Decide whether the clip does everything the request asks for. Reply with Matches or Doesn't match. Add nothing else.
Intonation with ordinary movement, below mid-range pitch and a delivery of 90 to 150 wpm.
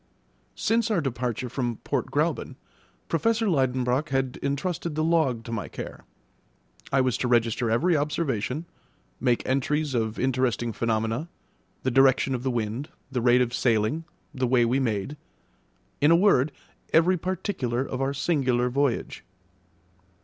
Matches